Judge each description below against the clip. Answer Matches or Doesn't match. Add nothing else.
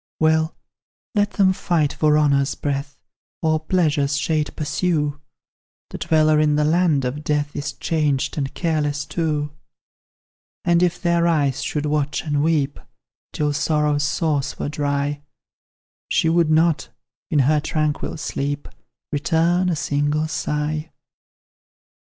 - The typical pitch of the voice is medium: Matches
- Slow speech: Matches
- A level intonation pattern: Matches